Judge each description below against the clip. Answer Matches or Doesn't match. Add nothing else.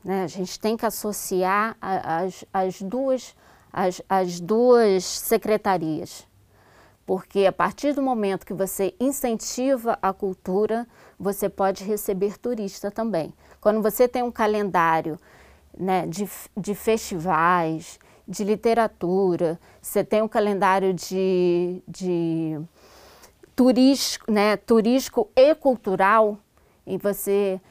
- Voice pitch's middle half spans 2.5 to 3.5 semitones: Matches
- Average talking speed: Doesn't match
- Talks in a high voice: Matches